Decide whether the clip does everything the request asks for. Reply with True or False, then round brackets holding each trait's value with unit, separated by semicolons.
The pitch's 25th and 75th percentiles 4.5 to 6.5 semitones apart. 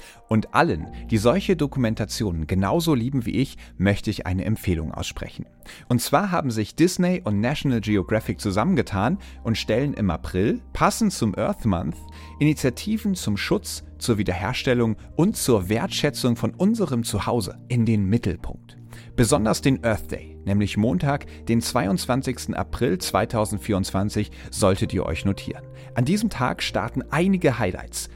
True (5.1 semitones)